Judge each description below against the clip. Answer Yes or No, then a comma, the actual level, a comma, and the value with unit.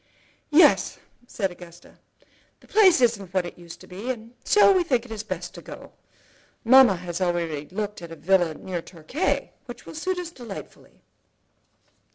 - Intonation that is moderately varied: No, wide, 6.6 semitones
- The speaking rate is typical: Yes, average, 165 wpm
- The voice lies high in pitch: Yes, high, 200 Hz